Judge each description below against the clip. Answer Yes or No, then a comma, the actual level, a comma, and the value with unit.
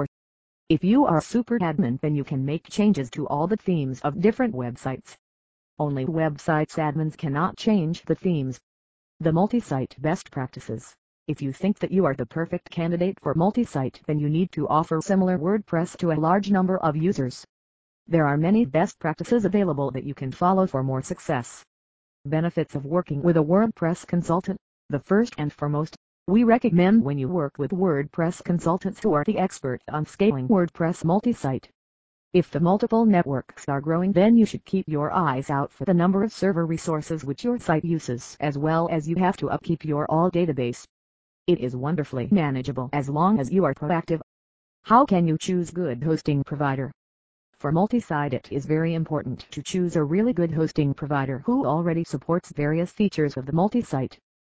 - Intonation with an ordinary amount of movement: Yes, average, 4.6 semitones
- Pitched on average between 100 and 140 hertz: No, medium, 160 Hz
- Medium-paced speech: Yes, average, 180 wpm